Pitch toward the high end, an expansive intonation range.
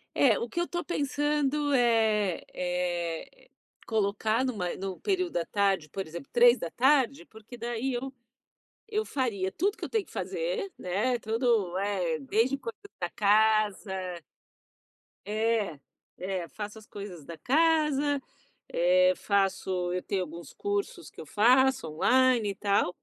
Yes: high, 220 Hz; wide, 6.2 semitones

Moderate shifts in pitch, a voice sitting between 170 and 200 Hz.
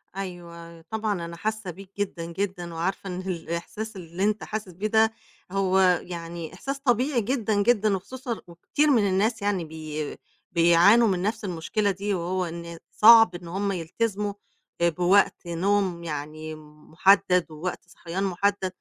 Yes: average, 3.5 semitones; medium, 185 Hz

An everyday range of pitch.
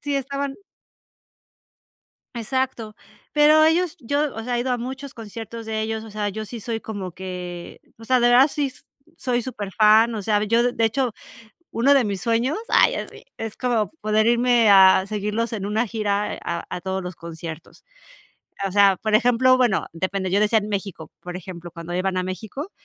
Yes: average, 4.0 semitones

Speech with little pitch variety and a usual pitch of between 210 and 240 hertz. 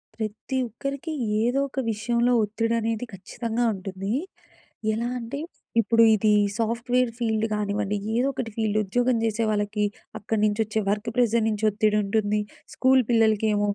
Yes: narrow, 2.2 semitones; high, 220 Hz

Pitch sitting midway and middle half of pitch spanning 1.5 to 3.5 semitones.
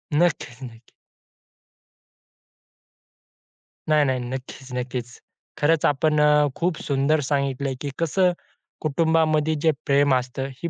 Yes: medium, 145 Hz; average, 2.9 semitones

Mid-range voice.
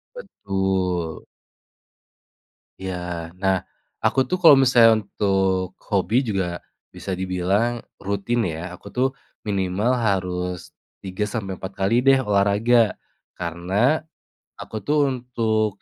No: low, 100 Hz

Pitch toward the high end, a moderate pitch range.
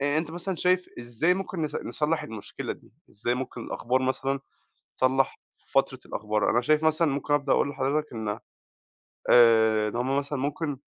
No: low, 135 Hz; average, 4.1 semitones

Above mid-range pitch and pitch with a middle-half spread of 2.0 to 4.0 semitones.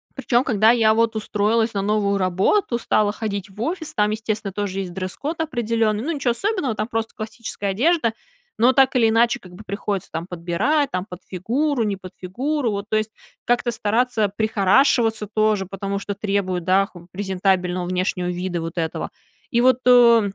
Yes: high, 215 Hz; average, 3.7 semitones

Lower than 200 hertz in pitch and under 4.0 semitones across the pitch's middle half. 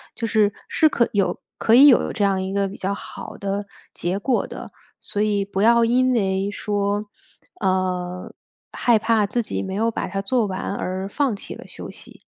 No: high, 205 Hz; average, 3.0 semitones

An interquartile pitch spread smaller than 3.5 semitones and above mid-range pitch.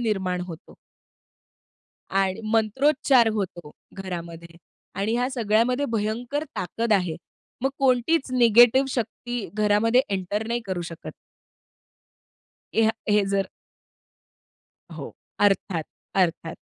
No: average, 4.3 semitones; high, 215 Hz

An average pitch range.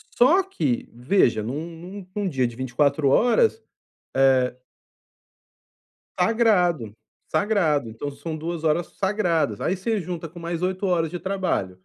No: wide, 6.1 semitones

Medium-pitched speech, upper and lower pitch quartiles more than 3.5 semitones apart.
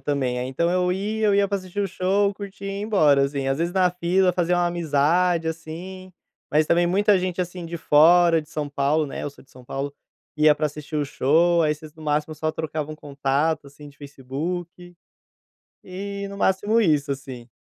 Yes: medium, 165 Hz; average, 3.9 semitones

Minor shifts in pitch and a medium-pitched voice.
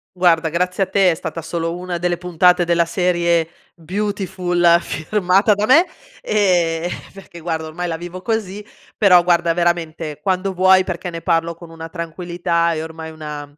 Yes: narrow, 1.8 semitones; medium, 175 Hz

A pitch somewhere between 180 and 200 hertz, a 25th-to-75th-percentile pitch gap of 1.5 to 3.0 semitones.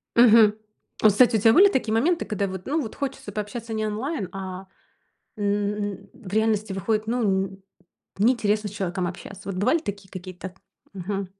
No: high, 210 Hz; average, 2.7 semitones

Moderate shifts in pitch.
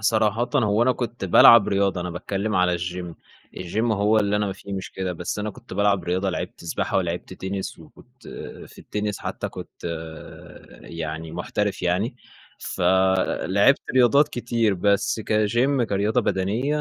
Yes: average, 3.2 semitones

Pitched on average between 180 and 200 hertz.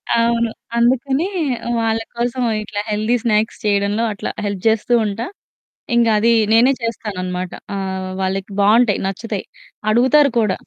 No: high, 220 Hz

